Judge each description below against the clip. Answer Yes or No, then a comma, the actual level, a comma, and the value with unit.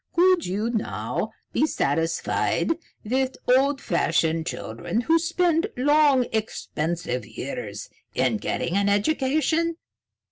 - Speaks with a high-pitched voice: Yes, very high, 255 Hz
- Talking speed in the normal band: No, slow, 105 wpm